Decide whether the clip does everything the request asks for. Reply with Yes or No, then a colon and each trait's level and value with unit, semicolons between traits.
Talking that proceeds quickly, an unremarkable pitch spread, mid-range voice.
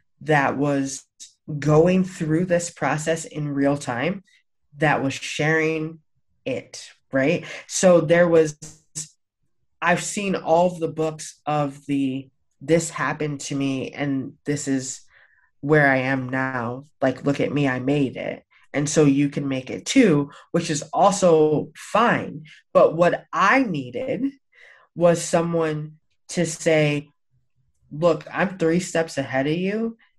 No: slow, 135 wpm; average, 3.3 semitones; medium, 155 Hz